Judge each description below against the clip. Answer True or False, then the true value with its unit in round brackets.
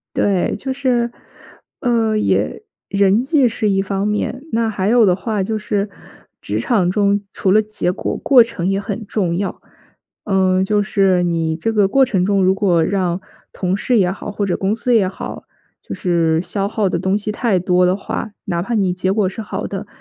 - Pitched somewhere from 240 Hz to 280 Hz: False (200 Hz)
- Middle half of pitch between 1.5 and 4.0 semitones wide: True (2.8 semitones)